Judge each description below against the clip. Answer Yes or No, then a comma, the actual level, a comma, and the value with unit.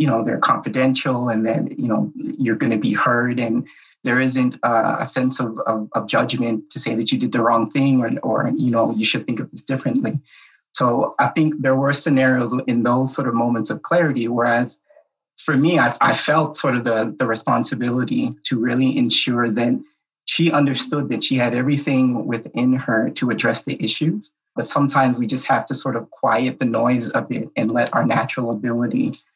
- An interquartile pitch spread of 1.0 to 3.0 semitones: Yes, average, 2.7 semitones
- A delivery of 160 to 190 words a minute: No, average, 200 wpm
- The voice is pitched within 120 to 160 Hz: Yes, low, 125 Hz